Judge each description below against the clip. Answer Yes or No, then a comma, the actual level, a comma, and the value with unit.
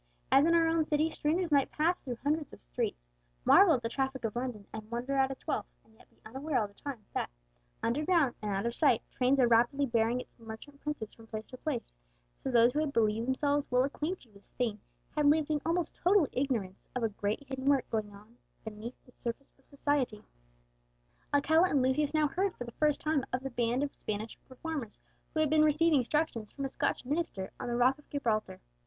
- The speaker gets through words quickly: Yes, fast, 215 wpm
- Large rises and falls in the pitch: No, average, 4.6 semitones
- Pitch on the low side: No, very high, 265 Hz